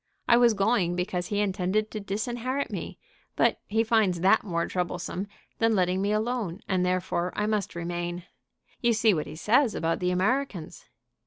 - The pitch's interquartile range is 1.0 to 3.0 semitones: No, average, 3.7 semitones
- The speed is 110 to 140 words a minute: No, average, 170 wpm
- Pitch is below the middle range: No, high, 195 Hz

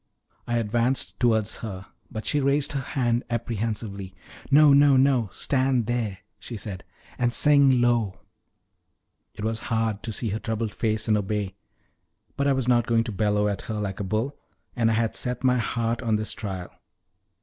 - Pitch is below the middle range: Yes, low, 115 Hz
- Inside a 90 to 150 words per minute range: No, average, 175 wpm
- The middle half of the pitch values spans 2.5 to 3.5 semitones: Yes, average, 2.8 semitones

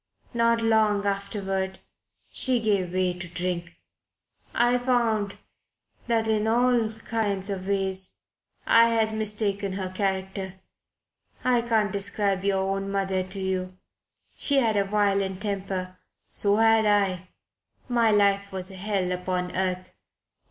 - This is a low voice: No, high, 200 Hz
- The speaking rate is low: Yes, slow, 130 wpm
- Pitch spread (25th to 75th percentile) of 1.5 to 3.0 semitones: Yes, narrow, 2.5 semitones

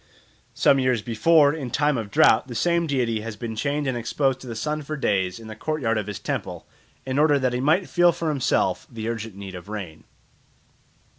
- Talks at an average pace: No, fast, 210 wpm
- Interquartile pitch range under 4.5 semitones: No, average, 5.1 semitones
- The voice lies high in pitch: No, low, 125 Hz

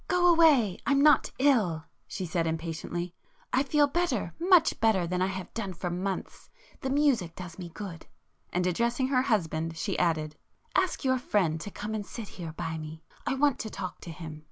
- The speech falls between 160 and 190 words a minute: Yes, average, 165 wpm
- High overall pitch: Yes, high, 195 Hz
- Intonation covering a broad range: Yes, wide, 7.9 semitones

